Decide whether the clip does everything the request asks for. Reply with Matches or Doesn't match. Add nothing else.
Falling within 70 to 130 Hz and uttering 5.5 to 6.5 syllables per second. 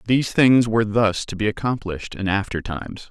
Matches